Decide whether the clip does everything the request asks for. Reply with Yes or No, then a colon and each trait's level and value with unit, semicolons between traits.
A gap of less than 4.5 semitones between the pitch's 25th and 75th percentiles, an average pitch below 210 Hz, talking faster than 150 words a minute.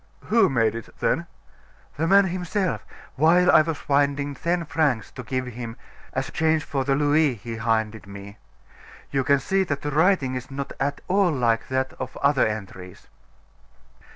No: average, 5.1 semitones; medium, 140 Hz; average, 165 wpm